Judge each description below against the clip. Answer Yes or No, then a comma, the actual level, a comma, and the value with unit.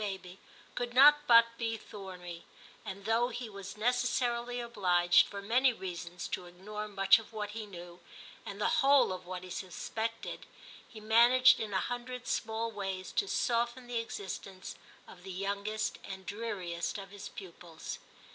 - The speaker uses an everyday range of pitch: Yes, average, 3.9 semitones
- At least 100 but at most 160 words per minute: Yes, average, 155 wpm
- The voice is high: Yes, high, 210 Hz